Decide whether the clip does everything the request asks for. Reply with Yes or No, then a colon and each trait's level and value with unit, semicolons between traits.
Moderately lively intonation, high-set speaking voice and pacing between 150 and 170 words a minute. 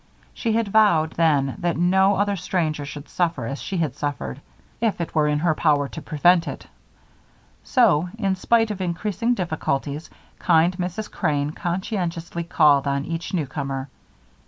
No: average, 4.2 semitones; medium, 170 Hz; average, 155 wpm